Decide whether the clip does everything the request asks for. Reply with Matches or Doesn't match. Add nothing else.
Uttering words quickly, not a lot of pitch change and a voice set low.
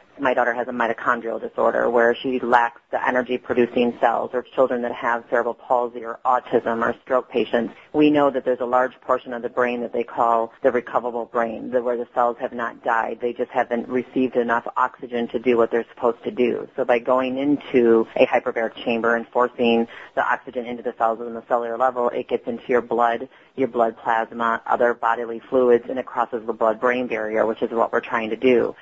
Matches